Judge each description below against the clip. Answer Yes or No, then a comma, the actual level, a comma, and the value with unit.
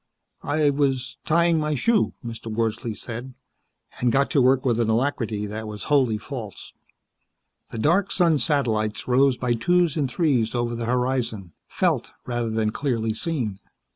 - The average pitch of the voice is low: Yes, low, 125 Hz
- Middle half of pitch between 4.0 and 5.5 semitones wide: Yes, average, 4.3 semitones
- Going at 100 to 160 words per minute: Yes, average, 155 wpm